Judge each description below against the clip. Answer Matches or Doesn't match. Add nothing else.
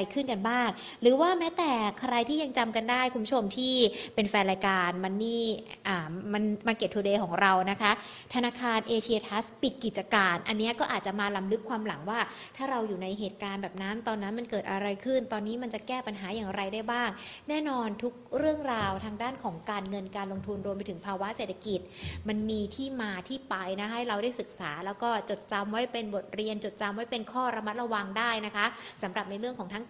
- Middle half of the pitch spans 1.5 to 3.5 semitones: Matches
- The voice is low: Doesn't match